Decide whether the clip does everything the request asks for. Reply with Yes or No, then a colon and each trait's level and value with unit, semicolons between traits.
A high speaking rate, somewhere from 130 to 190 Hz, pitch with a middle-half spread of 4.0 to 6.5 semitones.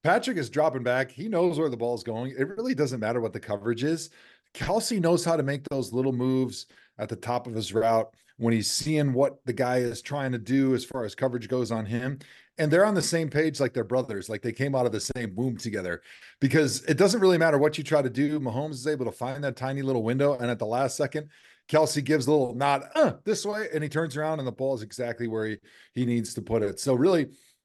Yes: fast, 255 wpm; low, 135 Hz; average, 4.4 semitones